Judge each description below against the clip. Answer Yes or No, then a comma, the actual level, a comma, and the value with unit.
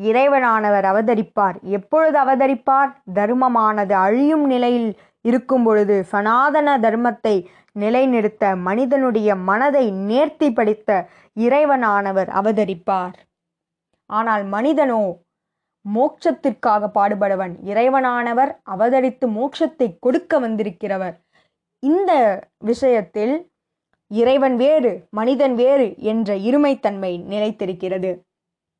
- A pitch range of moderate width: Yes, average, 5.0 semitones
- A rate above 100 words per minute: No, slow, 75 wpm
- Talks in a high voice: Yes, high, 225 Hz